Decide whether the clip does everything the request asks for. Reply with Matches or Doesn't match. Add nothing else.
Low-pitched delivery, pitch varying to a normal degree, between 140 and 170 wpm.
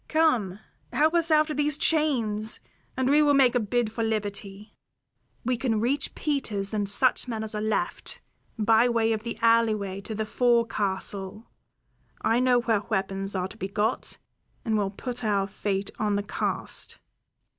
Doesn't match